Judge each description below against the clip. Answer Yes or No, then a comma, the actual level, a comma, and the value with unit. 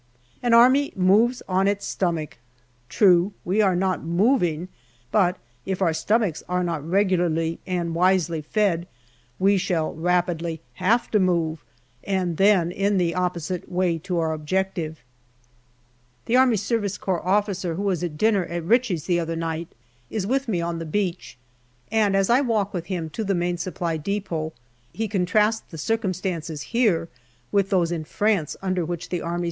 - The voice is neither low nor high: Yes, medium, 180 Hz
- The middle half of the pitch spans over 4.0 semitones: No, average, 3.2 semitones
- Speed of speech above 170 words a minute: No, average, 165 wpm